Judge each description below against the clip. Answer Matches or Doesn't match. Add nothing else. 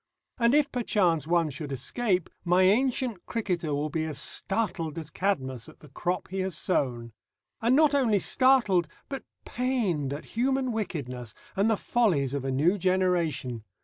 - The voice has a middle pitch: Matches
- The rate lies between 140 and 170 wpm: Matches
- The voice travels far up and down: Matches